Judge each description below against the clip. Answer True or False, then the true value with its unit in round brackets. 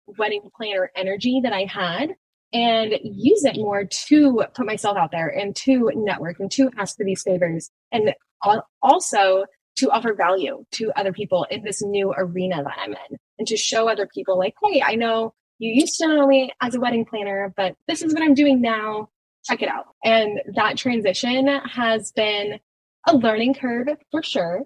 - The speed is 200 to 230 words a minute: False (185 wpm)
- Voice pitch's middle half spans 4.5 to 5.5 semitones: True (4.9 semitones)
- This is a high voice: True (215 Hz)